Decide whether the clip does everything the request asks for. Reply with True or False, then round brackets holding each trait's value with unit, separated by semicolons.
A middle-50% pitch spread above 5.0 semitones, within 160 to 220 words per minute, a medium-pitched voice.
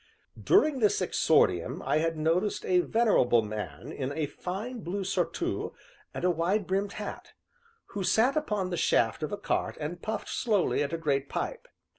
True (5.4 semitones; 170 wpm; 180 Hz)